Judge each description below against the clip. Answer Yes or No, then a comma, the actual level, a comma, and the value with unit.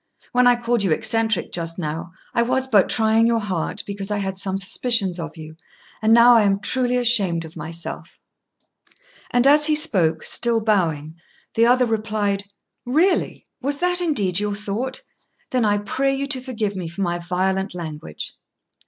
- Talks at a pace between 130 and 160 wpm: No, average, 170 wpm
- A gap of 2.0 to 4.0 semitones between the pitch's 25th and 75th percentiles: No, average, 5.2 semitones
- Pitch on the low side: No, high, 210 Hz